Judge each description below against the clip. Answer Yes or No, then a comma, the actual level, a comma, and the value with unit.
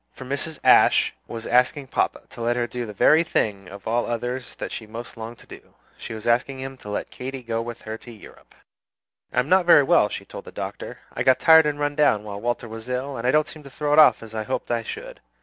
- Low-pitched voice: Yes, low, 125 Hz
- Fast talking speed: Yes, fast, 255 wpm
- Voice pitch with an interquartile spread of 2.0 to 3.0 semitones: No, average, 3.7 semitones